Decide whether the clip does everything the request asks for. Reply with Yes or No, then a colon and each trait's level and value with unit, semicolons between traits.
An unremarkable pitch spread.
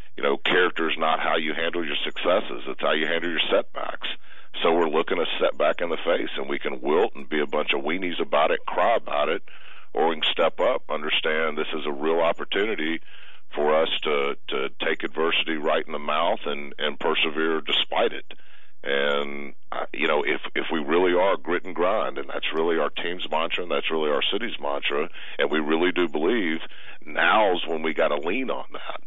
No: narrow, 2.0 semitones